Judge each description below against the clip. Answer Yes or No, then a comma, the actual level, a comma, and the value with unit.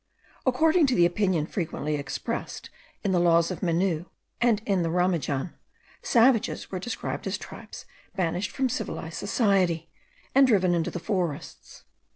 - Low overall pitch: No, medium, 185 Hz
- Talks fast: No, average, 145 wpm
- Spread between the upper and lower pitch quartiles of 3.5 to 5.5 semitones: Yes, average, 4.5 semitones